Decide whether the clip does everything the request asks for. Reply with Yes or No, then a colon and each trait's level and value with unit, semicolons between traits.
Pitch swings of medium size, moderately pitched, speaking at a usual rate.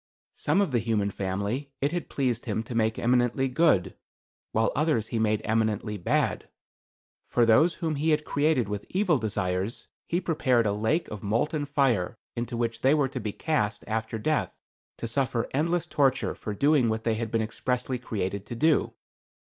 No: average, 4.8 semitones; low, 120 Hz; average, 180 wpm